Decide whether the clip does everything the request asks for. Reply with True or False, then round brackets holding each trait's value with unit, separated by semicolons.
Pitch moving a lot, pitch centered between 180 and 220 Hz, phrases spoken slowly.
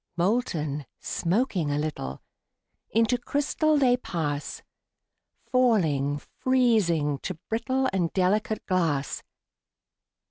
True (8.6 semitones; 185 Hz; 85 wpm)